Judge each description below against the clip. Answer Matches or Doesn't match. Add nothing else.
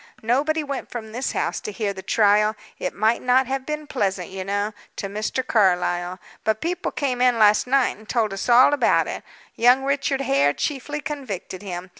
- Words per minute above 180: Matches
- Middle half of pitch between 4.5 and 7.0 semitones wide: Matches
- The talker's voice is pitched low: Doesn't match